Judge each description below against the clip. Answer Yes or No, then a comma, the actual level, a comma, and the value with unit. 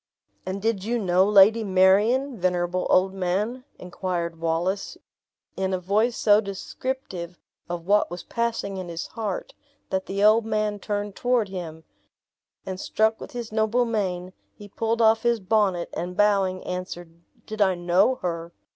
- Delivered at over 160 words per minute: No, average, 155 wpm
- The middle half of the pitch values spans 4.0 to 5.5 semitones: No, average, 3.3 semitones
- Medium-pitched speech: No, high, 195 Hz